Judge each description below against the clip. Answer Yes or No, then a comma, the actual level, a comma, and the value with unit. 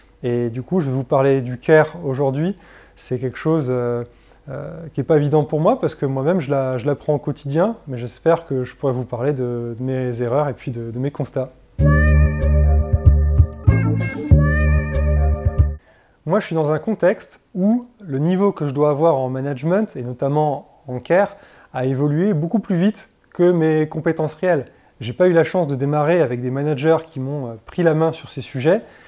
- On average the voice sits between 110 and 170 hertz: Yes, medium, 140 Hz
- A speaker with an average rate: Yes, average, 190 wpm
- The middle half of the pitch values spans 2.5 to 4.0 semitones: No, average, 4.7 semitones